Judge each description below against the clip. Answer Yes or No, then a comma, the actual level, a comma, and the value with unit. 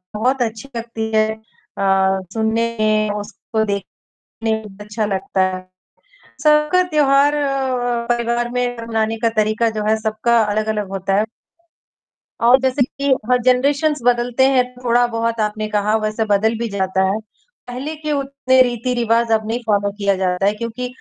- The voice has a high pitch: Yes, high, 225 Hz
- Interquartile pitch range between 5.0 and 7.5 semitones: No, average, 2.8 semitones